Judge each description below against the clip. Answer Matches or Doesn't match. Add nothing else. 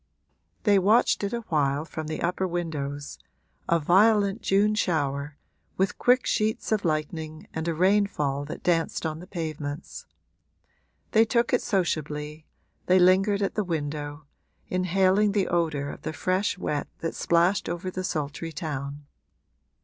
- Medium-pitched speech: Matches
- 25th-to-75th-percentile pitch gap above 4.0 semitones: Matches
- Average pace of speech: Matches